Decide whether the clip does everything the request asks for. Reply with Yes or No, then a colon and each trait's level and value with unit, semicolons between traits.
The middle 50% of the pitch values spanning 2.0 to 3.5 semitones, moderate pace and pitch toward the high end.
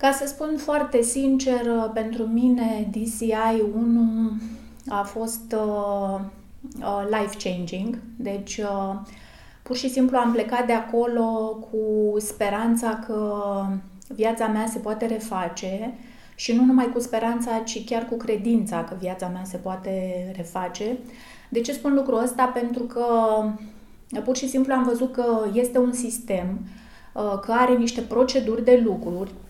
Yes: narrow, 2.5 semitones; average, 140 wpm; high, 225 Hz